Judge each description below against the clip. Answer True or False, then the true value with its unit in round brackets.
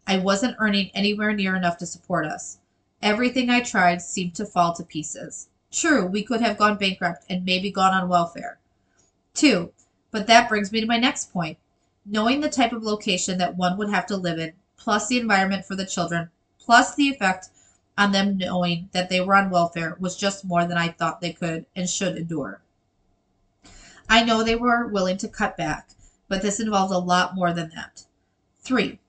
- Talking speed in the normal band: True (195 wpm)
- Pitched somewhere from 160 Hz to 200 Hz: True (190 Hz)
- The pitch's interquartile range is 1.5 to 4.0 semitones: True (3.7 semitones)